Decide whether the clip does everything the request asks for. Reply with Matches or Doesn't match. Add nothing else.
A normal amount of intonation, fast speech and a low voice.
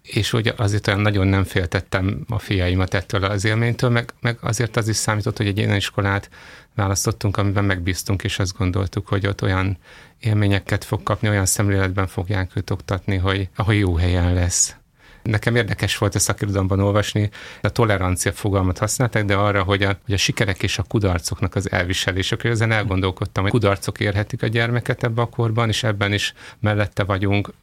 Doesn't match